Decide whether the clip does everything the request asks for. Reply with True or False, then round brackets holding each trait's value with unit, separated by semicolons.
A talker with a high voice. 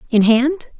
True (260 Hz)